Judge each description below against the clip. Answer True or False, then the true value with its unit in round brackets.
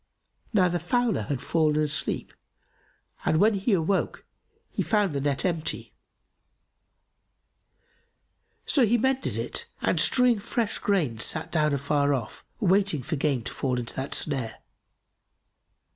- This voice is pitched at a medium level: True (155 Hz)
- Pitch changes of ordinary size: False (6.5 semitones)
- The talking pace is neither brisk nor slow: False (130 wpm)